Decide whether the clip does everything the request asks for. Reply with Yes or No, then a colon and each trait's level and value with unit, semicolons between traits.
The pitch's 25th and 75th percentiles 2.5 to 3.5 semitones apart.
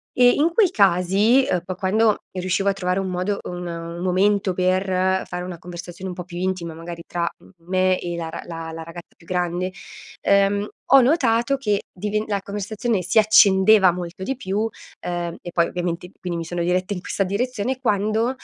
Yes: average, 2.9 semitones